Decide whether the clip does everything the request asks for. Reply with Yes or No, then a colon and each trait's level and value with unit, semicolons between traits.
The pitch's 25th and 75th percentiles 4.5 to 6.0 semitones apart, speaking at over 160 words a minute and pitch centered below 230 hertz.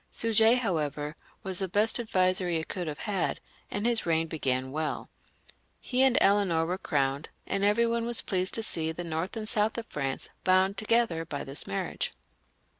Yes: wide, 5.5 semitones; average, 180 wpm; medium, 185 Hz